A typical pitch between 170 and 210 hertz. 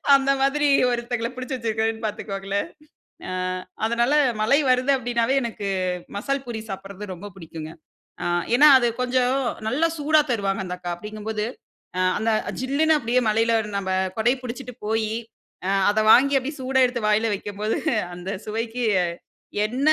No: high, 230 Hz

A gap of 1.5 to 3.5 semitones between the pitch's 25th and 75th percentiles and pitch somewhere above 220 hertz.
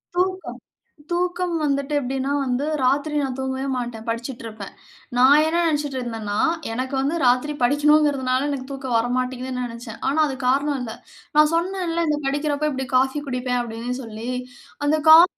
Yes: average, 3.2 semitones; very high, 270 Hz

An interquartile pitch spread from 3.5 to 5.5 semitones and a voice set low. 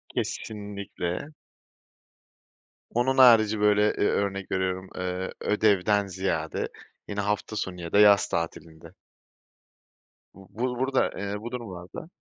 No: narrow, 2.6 semitones; low, 100 Hz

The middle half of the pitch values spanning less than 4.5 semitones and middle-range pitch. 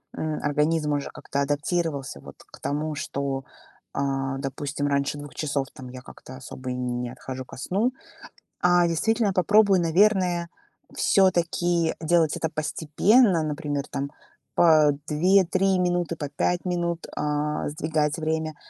Yes: average, 3.7 semitones; medium, 155 Hz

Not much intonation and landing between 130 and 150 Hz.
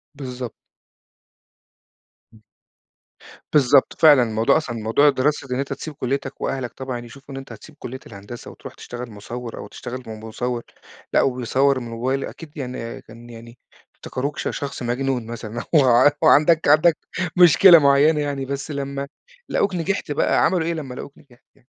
No: average, 3.3 semitones; low, 135 Hz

